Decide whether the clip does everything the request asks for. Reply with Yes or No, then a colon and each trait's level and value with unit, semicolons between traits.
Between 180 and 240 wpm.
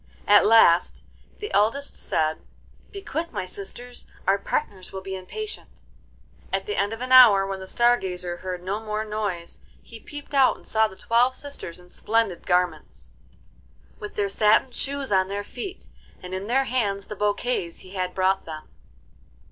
No: average, 170 wpm